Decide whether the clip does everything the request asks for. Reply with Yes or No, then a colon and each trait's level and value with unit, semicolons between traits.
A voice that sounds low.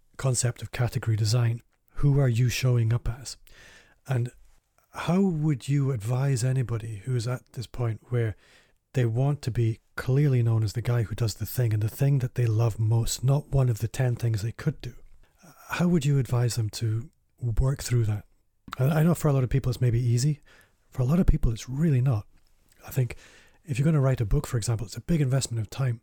Yes: low, 120 Hz